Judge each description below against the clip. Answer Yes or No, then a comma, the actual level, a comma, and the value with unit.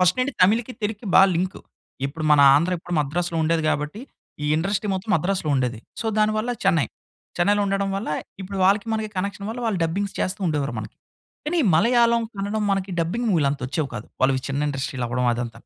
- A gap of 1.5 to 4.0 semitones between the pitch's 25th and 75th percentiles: No, wide, 5.6 semitones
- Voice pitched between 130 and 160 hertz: No, medium, 185 Hz